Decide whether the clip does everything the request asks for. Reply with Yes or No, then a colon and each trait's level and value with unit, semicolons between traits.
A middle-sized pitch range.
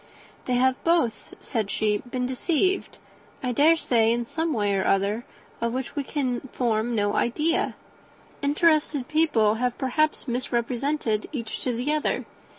Yes: average, 4.6 semitones